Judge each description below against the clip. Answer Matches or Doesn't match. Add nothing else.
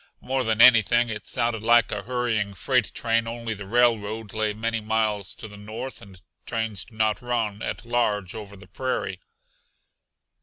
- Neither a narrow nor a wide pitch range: Doesn't match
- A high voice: Doesn't match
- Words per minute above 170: Doesn't match